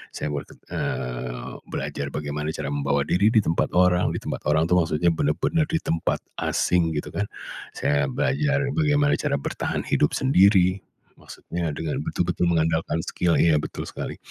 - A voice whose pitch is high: No, very low, 85 Hz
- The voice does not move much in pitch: No, average, 4.3 semitones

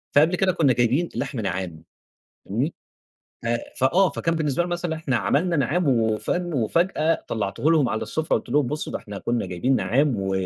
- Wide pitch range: Yes, wide, 6.3 semitones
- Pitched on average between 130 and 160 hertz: Yes, medium, 140 Hz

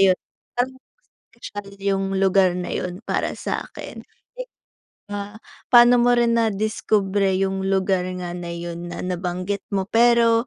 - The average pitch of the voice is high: Yes, high, 195 Hz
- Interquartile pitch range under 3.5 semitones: No, average, 3.8 semitones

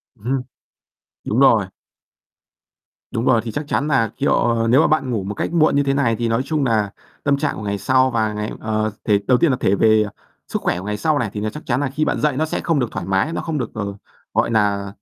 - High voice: No, low, 120 Hz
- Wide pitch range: No, average, 4.7 semitones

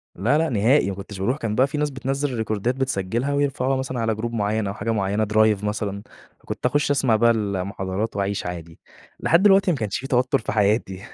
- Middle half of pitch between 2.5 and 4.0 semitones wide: No, average, 4.8 semitones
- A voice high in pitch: No, low, 110 Hz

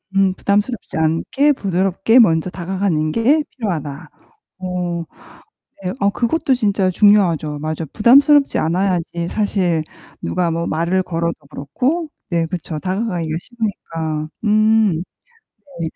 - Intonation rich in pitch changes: No, average, 4.7 semitones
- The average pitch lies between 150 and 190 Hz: Yes, medium, 185 Hz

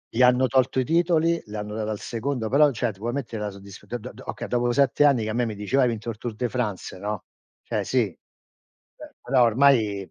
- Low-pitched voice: Yes, low, 120 Hz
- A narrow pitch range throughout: No, average, 3.6 semitones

